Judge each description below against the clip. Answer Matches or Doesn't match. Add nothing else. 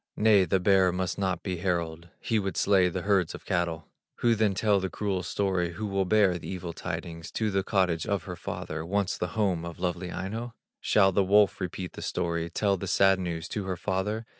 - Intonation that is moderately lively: Doesn't match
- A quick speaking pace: Matches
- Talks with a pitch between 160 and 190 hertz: Doesn't match